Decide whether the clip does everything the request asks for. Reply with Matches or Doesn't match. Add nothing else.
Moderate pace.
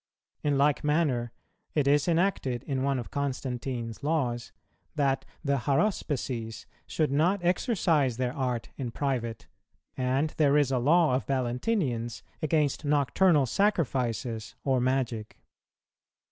Doesn't match